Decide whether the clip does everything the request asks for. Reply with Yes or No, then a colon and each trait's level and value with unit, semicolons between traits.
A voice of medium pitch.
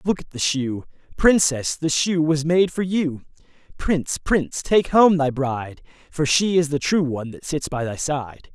Yes: medium, 155 Hz